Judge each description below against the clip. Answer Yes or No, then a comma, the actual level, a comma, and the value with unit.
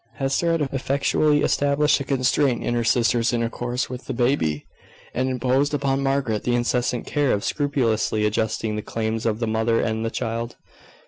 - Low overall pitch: Yes, low, 120 Hz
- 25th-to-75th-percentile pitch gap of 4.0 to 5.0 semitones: No, average, 3.4 semitones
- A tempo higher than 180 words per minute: No, average, 170 wpm